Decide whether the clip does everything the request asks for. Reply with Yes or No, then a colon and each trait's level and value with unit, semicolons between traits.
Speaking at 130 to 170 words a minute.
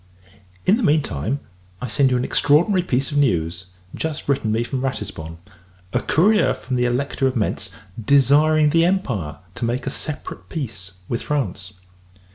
Yes: average, 165 wpm